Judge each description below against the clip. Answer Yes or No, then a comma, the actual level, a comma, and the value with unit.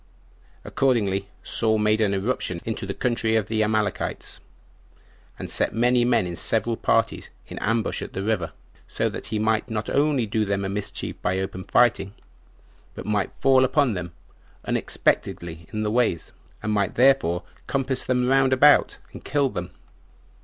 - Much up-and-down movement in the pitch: No, average, 4.2 semitones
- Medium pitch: No, low, 110 Hz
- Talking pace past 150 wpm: Yes, average, 160 wpm